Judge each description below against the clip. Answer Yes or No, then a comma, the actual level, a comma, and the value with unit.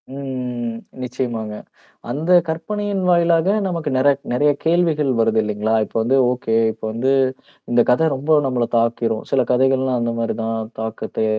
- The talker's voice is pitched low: Yes, low, 125 Hz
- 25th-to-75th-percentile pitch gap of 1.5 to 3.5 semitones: No, average, 4.8 semitones